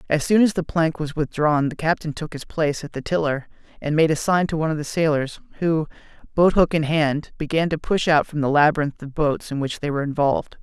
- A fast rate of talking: Yes, fast, 245 wpm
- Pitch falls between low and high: Yes, medium, 155 Hz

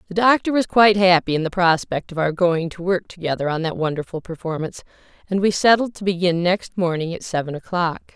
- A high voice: No, medium, 180 Hz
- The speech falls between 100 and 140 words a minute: No, fast, 205 wpm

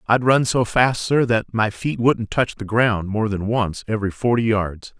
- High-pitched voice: No, low, 110 Hz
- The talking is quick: Yes, fast, 215 wpm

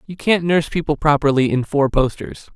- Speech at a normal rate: Yes, average, 190 wpm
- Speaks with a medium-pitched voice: Yes, medium, 150 Hz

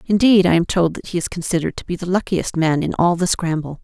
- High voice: No, medium, 175 Hz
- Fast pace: Yes, fast, 265 wpm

